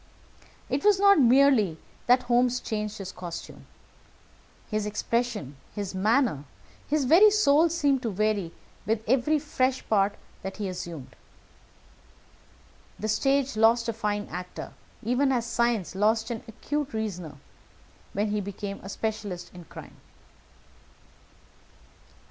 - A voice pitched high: Yes, high, 220 Hz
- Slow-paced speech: Yes, slow, 125 wpm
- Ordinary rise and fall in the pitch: Yes, average, 4.4 semitones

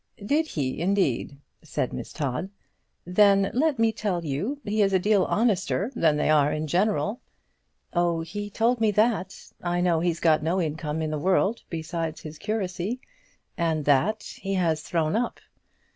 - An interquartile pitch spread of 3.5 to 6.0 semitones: Yes, average, 4.8 semitones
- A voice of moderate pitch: Yes, medium, 180 Hz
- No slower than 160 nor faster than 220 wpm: Yes, average, 165 wpm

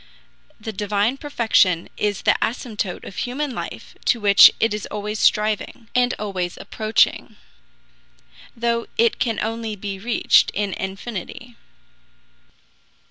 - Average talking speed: No, slow, 120 wpm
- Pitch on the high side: Yes, high, 215 Hz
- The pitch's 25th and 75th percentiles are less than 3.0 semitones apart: Yes, narrow, 2.4 semitones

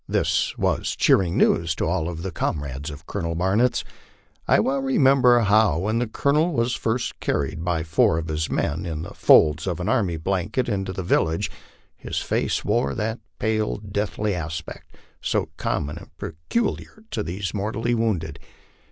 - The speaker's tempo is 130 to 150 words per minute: No, average, 165 wpm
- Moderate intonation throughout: No, wide, 5.8 semitones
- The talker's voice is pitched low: Yes, very low, 95 Hz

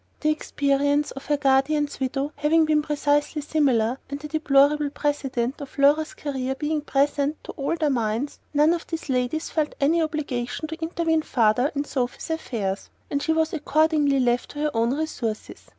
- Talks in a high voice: Yes, very high, 290 Hz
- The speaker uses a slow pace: No, average, 170 wpm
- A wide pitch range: No, narrow, 2.5 semitones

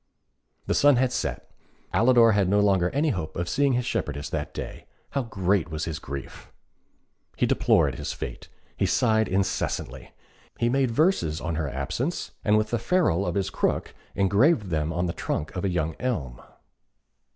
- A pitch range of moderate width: No, wide, 6.9 semitones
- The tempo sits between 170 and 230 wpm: Yes, average, 175 wpm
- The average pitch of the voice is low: Yes, very low, 95 Hz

